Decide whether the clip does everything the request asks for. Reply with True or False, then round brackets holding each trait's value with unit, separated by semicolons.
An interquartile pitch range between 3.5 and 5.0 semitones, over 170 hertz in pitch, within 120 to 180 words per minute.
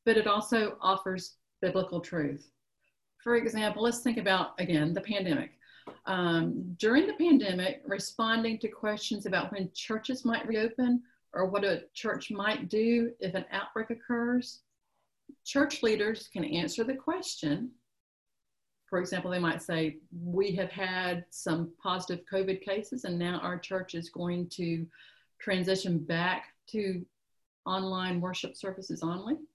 True (4.2 semitones; 190 Hz; 140 wpm)